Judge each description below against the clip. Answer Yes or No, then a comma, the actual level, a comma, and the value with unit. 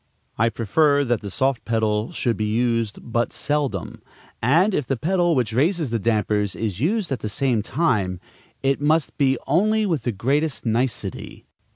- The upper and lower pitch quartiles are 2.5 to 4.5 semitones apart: No, average, 5.2 semitones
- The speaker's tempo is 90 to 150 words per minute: No, average, 170 wpm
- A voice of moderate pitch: No, low, 125 Hz